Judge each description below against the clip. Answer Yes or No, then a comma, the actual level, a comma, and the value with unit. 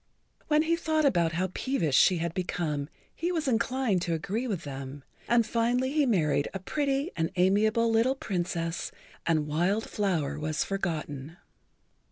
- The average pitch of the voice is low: No, high, 190 Hz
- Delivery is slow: No, average, 155 wpm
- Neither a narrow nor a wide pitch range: No, wide, 7.2 semitones